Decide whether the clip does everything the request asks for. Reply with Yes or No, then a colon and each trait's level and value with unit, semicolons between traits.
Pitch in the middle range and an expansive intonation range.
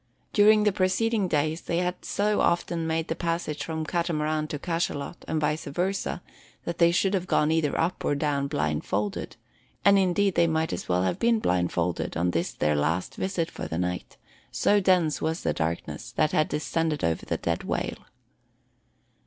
No: medium, 160 Hz; average, 4.2 semitones